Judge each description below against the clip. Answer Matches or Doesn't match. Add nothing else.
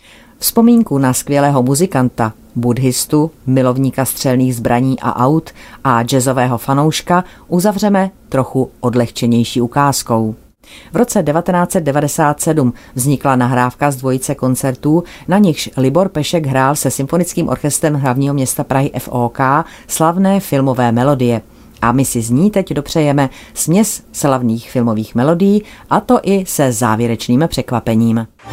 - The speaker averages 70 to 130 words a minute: Matches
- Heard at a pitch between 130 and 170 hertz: Matches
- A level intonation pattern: Doesn't match